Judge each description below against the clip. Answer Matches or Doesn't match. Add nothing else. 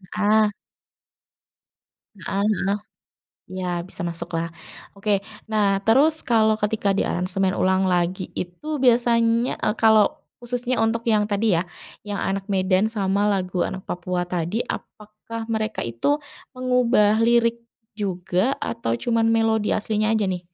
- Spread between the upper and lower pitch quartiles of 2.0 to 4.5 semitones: Matches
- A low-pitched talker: Doesn't match